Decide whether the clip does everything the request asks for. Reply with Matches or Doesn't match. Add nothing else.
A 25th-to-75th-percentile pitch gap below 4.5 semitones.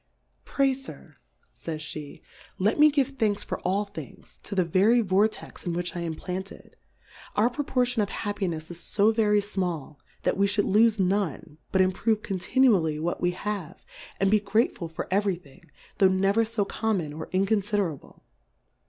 Matches